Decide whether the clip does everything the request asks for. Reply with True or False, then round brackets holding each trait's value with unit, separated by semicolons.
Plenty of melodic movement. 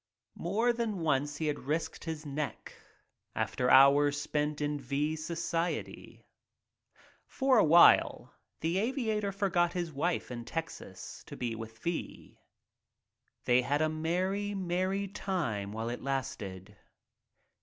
False (5.0 semitones)